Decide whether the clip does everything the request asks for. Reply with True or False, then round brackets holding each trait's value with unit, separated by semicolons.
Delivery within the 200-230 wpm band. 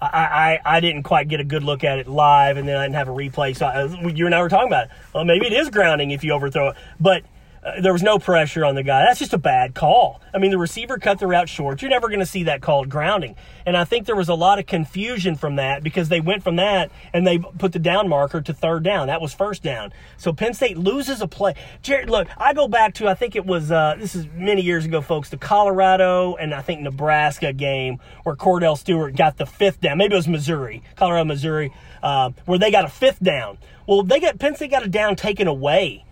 False (260 wpm)